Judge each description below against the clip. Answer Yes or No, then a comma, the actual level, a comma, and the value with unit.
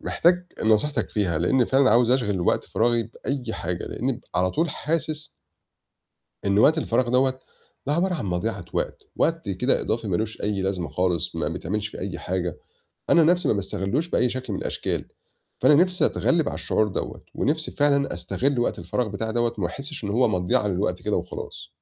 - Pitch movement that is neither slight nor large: No, wide, 6.6 semitones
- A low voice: Yes, low, 115 Hz